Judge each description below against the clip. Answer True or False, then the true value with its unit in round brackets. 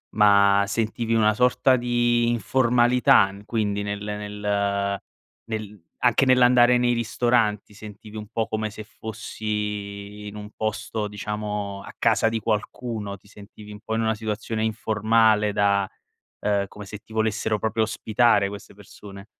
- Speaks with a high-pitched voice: False (105 Hz)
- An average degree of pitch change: False (1.7 semitones)